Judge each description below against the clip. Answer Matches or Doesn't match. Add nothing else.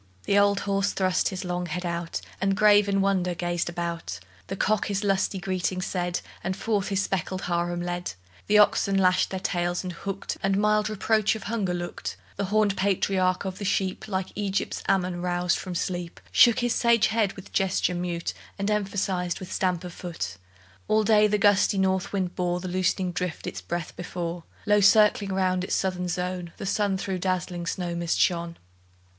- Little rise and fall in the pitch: Matches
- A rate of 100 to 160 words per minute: Doesn't match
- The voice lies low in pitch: Doesn't match